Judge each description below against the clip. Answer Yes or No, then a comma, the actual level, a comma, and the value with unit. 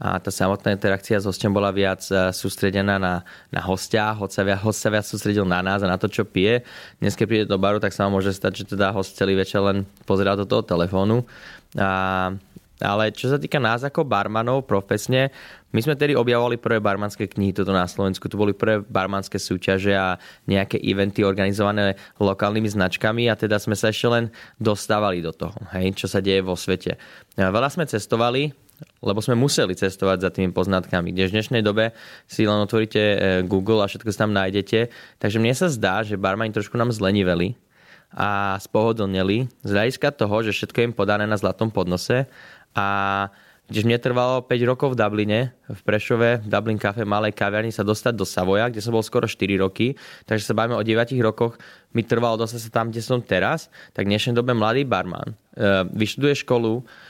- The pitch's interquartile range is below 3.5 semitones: Yes, average, 2.9 semitones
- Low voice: Yes, low, 105 Hz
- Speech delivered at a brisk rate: Yes, fast, 190 wpm